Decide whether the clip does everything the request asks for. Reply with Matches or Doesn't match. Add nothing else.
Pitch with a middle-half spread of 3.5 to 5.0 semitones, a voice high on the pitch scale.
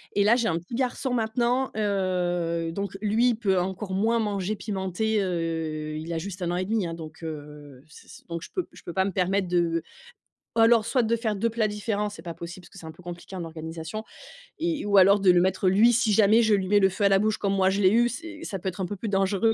Matches